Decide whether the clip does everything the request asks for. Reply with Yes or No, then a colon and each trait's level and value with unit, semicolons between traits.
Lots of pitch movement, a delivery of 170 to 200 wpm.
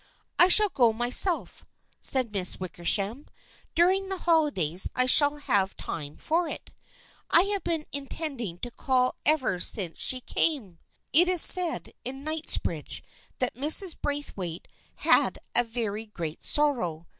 No: wide, 7.9 semitones; average, 145 wpm